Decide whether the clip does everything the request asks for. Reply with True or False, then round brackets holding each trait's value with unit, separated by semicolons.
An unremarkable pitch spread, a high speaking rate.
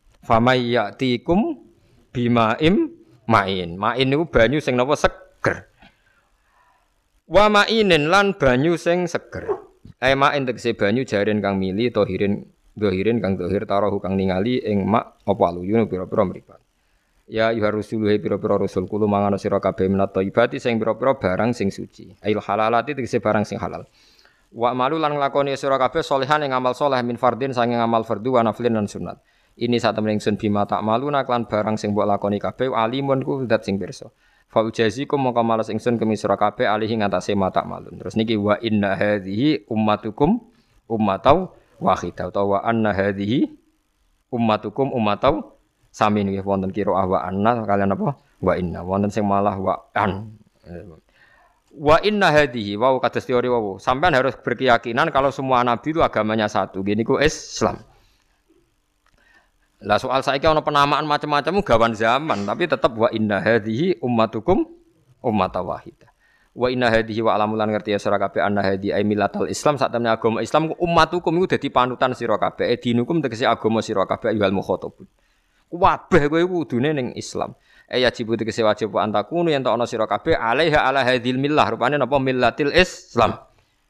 True (4.6 semitones; 160 wpm)